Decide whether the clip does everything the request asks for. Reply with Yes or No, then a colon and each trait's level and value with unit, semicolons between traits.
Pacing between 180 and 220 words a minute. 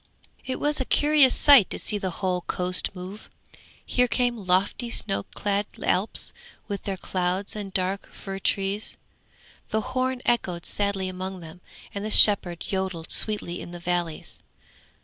No: average, 150 wpm